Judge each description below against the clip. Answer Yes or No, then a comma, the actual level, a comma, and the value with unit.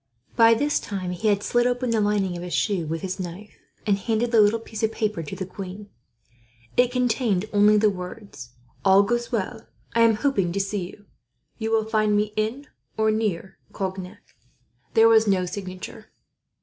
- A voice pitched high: Yes, high, 210 Hz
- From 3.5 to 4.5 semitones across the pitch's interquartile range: No, average, 2.9 semitones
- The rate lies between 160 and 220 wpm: Yes, average, 180 wpm